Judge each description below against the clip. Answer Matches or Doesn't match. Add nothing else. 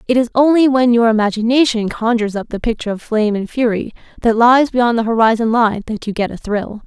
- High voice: Matches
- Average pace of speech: Doesn't match